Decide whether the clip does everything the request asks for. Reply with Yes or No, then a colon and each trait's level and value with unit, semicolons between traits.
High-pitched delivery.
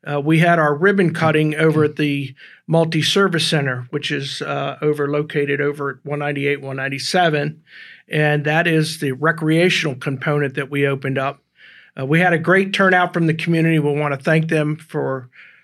No: medium, 150 Hz